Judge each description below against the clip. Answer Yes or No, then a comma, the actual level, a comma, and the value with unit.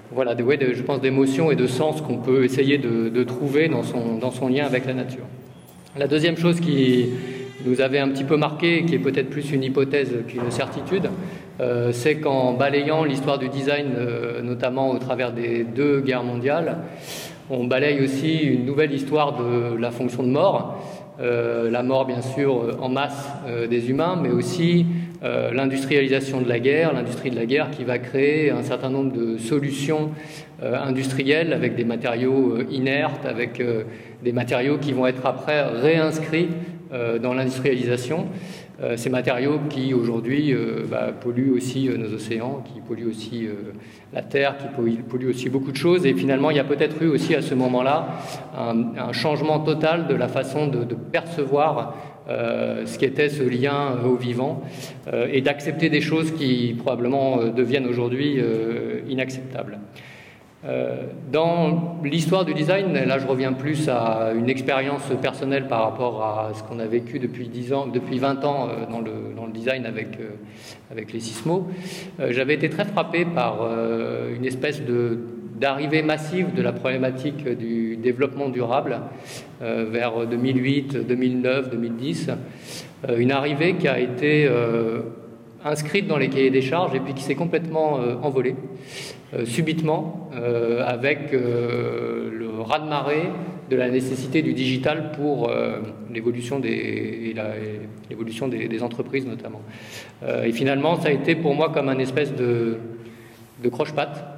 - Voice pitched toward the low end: Yes, low, 130 Hz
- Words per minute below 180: Yes, average, 170 wpm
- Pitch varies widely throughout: No, average, 3.5 semitones